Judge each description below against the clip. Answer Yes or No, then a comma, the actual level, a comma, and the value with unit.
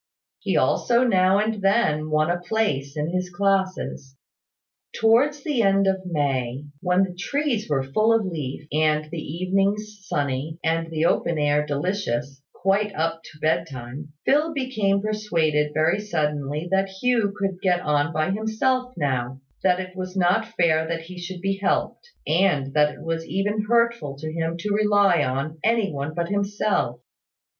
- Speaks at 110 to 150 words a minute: No, average, 160 wpm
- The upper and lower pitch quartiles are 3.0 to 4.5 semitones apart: No, average, 5.1 semitones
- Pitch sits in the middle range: Yes, medium, 180 Hz